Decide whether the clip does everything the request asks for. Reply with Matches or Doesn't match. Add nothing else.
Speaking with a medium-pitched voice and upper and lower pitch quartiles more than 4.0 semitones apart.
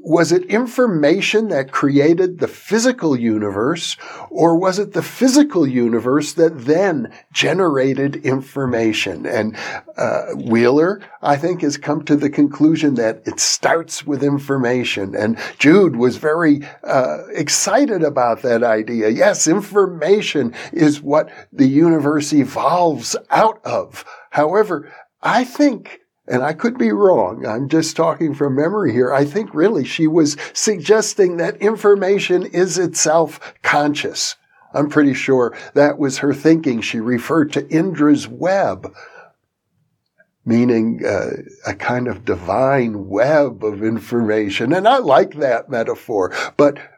Matches